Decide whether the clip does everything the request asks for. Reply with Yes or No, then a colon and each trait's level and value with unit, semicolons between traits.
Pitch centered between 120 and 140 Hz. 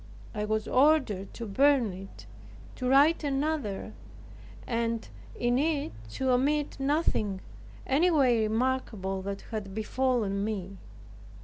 No: high, 240 Hz